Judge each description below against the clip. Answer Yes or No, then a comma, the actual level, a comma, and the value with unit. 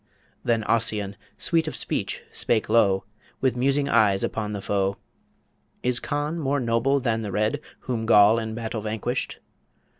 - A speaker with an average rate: Yes, average, 150 wpm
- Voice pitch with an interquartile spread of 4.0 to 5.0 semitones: No, average, 3.4 semitones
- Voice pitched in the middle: No, low, 115 Hz